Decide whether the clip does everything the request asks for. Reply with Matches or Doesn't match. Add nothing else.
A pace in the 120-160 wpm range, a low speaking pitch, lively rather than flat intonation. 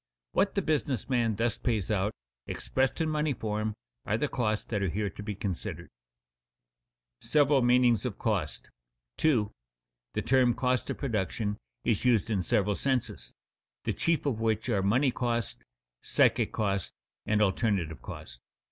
Doesn't match